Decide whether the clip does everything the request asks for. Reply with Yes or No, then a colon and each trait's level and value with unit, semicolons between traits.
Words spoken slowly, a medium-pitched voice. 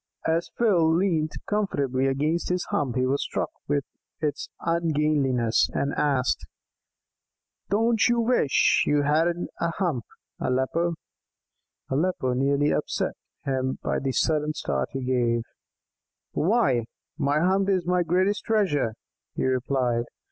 Yes: slow, 125 wpm; medium, 150 Hz